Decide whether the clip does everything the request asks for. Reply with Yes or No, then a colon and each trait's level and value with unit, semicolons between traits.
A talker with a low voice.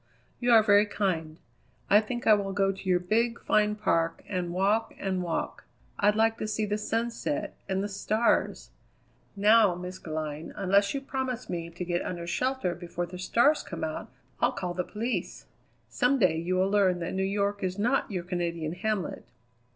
No: high, 195 Hz